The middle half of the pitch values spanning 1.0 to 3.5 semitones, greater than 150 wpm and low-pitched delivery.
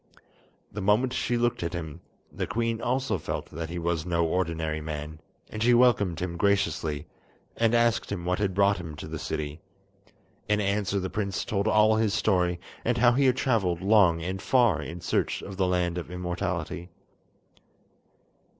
No: average, 4.3 semitones; average, 175 wpm; very low, 95 Hz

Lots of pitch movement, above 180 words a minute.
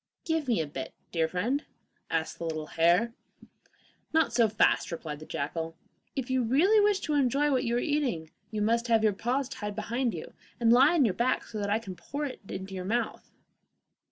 Yes: wide, 6.8 semitones; fast, 205 wpm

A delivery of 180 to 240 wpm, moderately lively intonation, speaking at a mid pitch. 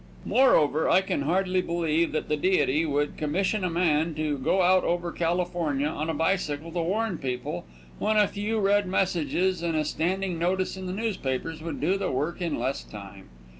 Yes: average, 185 wpm; average, 3.7 semitones; medium, 170 Hz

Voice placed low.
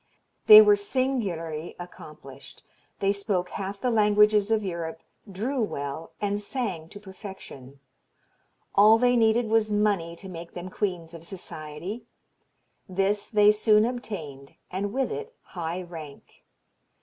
No: high, 200 Hz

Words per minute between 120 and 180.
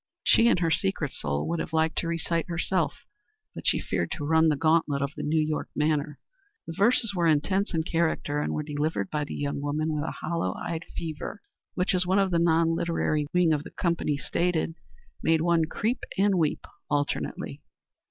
No: average, 195 wpm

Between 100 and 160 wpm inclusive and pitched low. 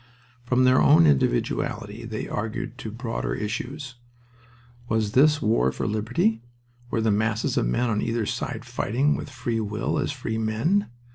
Yes: average, 155 wpm; low, 115 Hz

